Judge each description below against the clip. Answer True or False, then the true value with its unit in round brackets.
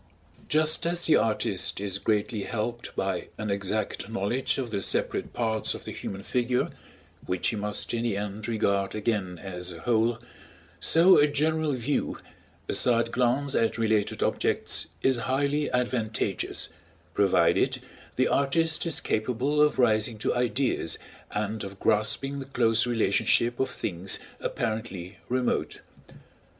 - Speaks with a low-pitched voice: True (115 Hz)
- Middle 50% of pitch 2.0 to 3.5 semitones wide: False (3.9 semitones)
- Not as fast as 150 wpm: True (140 wpm)